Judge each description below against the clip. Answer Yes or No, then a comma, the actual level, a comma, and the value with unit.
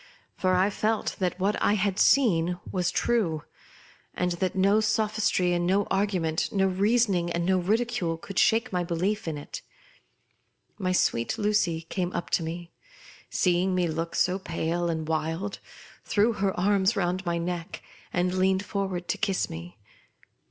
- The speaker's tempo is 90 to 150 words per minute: No, average, 160 wpm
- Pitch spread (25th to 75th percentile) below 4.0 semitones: Yes, average, 2.8 semitones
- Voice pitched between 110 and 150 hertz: No, medium, 185 Hz